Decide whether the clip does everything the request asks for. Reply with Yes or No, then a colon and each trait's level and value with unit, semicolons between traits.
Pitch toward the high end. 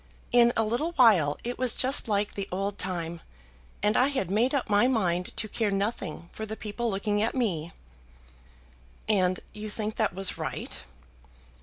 Yes: high, 210 Hz